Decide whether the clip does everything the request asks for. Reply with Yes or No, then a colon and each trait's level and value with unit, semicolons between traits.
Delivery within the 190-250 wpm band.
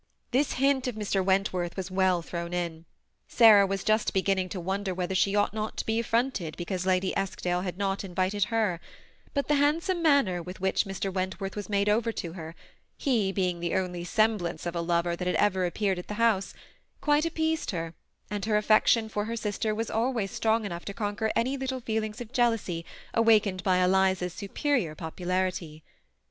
Yes: average, 195 wpm